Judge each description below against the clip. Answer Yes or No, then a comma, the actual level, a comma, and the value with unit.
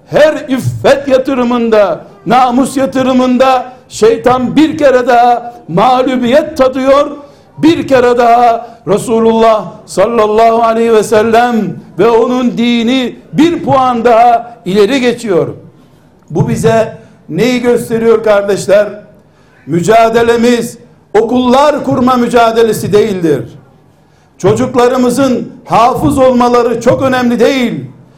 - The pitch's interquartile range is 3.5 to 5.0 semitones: No, average, 2.8 semitones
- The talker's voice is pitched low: No, high, 240 Hz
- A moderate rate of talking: No, slow, 90 wpm